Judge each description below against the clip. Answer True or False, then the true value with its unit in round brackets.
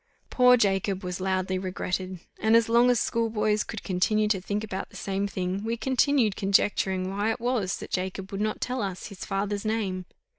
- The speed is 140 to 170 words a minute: False (190 wpm)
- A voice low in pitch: False (200 Hz)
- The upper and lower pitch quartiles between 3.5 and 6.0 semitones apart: False (2.8 semitones)